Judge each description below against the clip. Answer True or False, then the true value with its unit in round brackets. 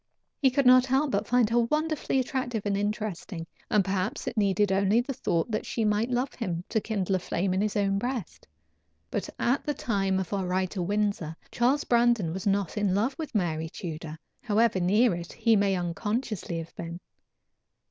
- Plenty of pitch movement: False (4.3 semitones)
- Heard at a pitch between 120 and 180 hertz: False (205 Hz)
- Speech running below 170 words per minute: False (190 wpm)